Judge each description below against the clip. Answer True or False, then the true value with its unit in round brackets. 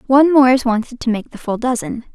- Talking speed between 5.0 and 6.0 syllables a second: False (6.3 syllables/s)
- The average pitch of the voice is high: True (245 Hz)